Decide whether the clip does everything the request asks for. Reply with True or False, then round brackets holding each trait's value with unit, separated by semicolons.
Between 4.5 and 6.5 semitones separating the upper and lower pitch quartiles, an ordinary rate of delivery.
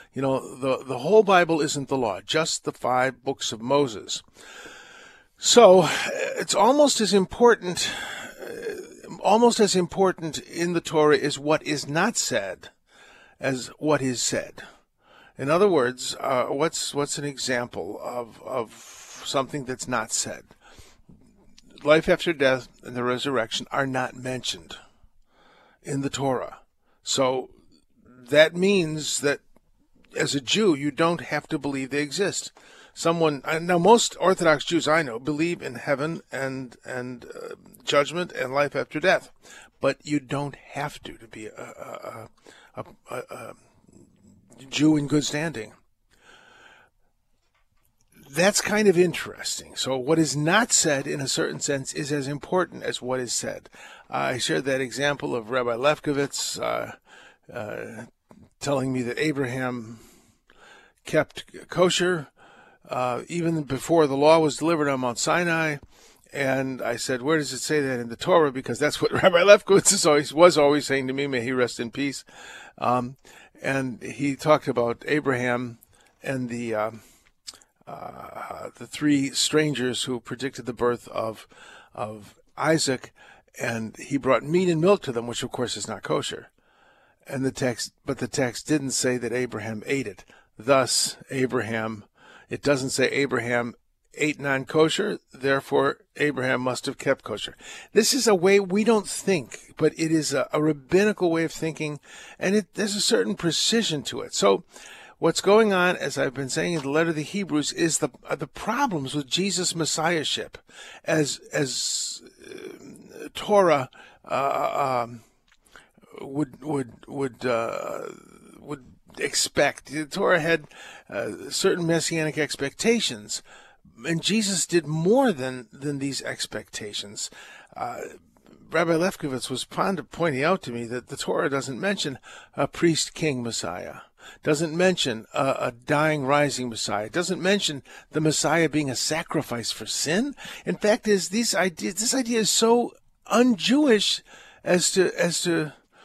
True (5.0 semitones; 150 wpm)